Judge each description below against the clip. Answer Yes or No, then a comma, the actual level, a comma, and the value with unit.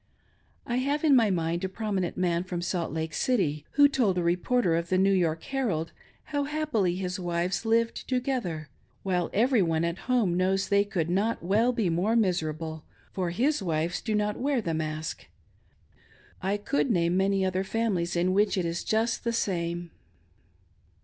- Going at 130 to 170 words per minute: No, average, 180 wpm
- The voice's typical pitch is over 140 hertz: Yes, high, 190 Hz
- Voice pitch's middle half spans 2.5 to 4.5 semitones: No, average, 5.0 semitones